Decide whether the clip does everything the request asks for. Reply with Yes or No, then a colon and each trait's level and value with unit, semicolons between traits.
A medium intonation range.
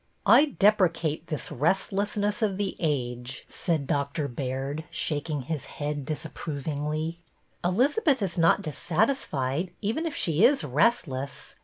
No: wide, 6.0 semitones